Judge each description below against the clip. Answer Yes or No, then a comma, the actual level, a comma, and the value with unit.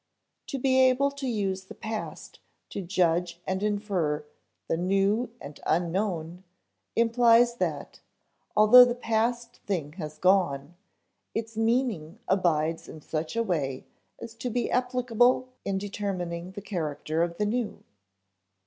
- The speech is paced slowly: Yes, slow, 130 wpm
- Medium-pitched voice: No, high, 200 Hz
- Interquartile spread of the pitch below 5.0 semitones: No, wide, 5.5 semitones